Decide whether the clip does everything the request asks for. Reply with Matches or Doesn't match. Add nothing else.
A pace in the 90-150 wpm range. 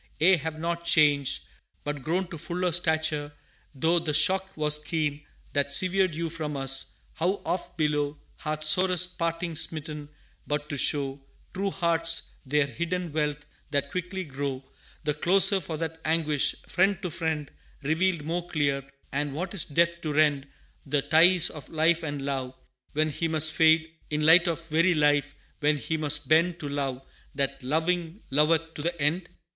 Doesn't match